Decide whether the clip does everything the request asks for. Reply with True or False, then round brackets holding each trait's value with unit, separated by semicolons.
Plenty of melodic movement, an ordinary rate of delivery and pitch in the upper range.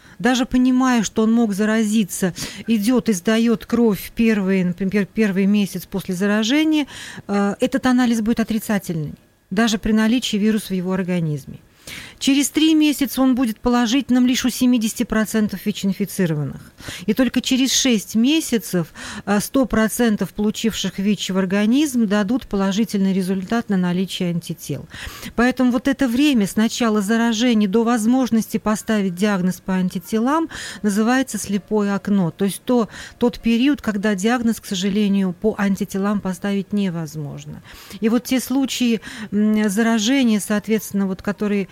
False (3.4 semitones; 130 wpm; 220 Hz)